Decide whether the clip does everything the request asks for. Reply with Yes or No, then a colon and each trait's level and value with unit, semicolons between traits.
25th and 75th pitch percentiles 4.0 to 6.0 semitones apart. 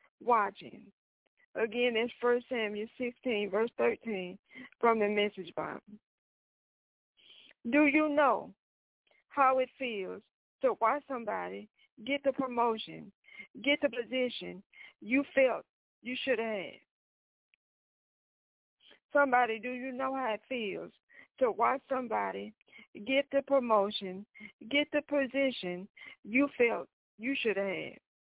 Yes: average, 4.3 semitones